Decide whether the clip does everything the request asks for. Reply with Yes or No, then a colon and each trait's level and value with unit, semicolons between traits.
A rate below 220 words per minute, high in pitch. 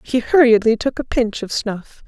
Yes: average, 200 wpm; high, 230 Hz